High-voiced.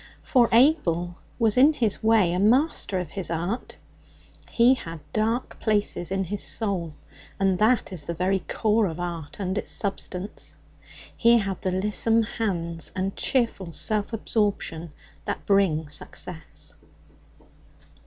Yes: high, 195 Hz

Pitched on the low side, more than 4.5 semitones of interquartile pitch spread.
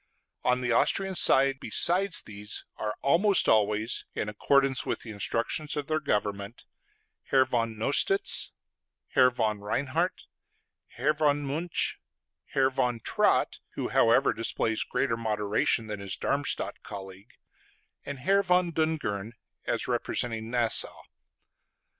Yes: low, 125 Hz; average, 5.2 semitones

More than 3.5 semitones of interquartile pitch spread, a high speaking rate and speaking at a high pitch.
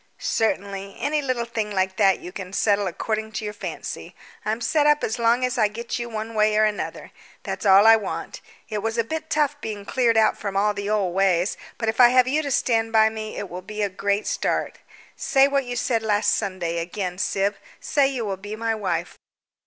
No: average, 2.9 semitones; fast, 220 wpm; high, 215 Hz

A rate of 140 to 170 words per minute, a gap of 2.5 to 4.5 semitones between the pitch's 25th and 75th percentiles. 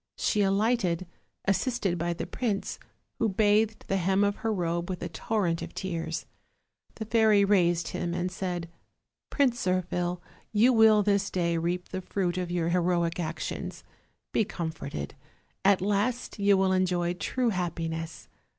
Yes: average, 150 wpm; average, 3.1 semitones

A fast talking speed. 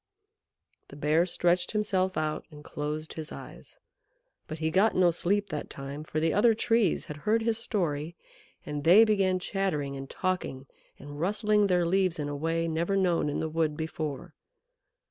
No: average, 170 wpm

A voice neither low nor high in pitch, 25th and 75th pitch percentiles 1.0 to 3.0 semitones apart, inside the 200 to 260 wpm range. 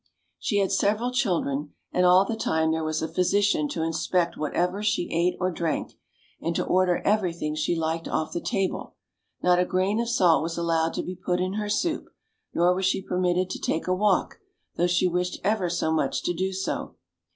Yes: medium, 180 Hz; narrow, 2.5 semitones; fast, 205 wpm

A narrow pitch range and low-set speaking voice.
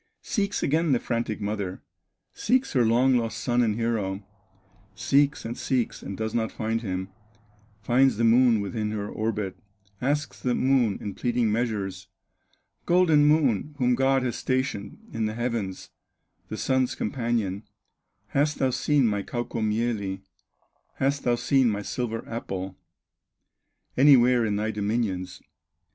No: average, 3.7 semitones; low, 115 Hz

